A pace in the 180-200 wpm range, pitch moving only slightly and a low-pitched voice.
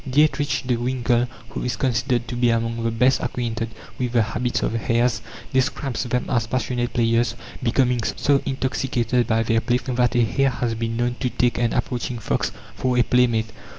Yes: average, 185 wpm; narrow, 1.5 semitones; low, 120 Hz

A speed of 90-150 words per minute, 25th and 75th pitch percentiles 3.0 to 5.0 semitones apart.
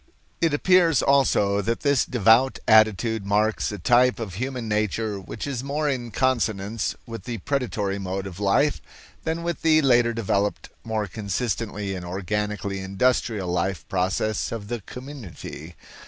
Yes: average, 145 wpm; average, 4.3 semitones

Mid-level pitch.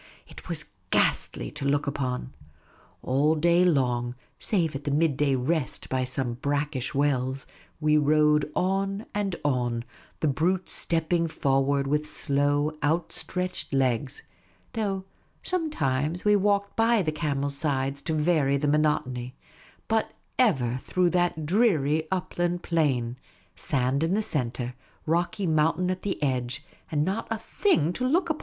Yes: medium, 150 Hz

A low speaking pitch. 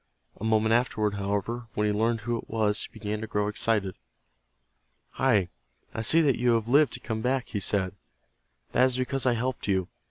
Yes: low, 110 Hz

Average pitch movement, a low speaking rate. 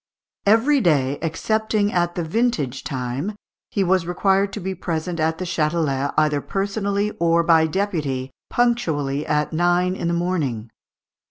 No: average, 4.6 semitones; average, 145 wpm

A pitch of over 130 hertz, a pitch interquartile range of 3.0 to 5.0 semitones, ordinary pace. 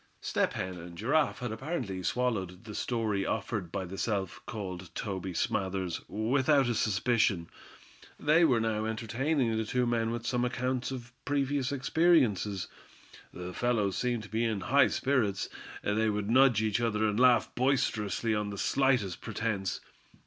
No: low, 110 Hz; average, 3.9 semitones; average, 155 wpm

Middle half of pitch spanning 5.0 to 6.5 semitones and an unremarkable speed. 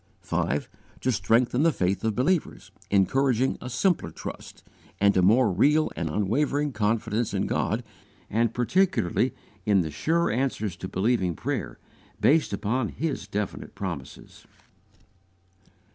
No: wide, 5.4 semitones; slow, 130 wpm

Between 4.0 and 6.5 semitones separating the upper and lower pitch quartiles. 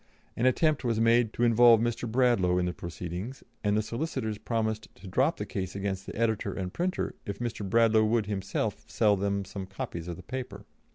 No: average, 3.4 semitones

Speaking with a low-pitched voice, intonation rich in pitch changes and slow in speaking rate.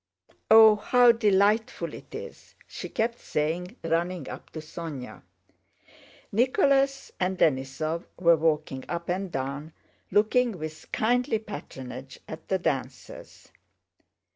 No: medium, 175 Hz; wide, 6.0 semitones; slow, 115 wpm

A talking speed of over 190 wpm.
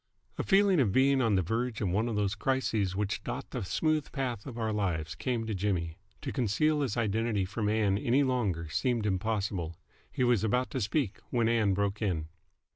Yes: average, 200 wpm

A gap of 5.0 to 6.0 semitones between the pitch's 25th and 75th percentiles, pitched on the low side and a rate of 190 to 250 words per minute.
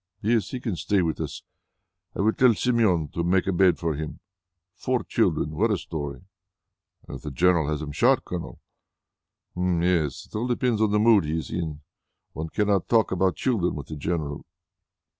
Yes: average, 5.3 semitones; very low, 90 Hz; average, 195 wpm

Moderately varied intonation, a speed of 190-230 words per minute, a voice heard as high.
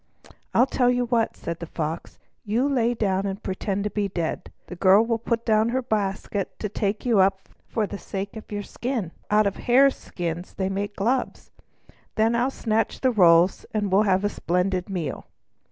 Yes: average, 3.3 semitones; average, 200 wpm; high, 205 Hz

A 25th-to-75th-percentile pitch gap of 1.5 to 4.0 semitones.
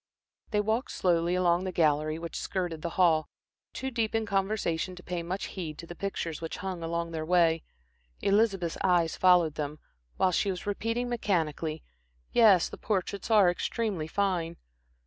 Yes: average, 3.3 semitones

